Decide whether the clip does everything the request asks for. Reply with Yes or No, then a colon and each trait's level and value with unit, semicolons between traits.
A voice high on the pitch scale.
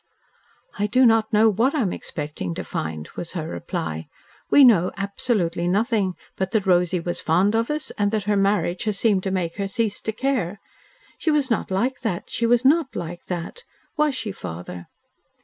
Yes: high, 200 Hz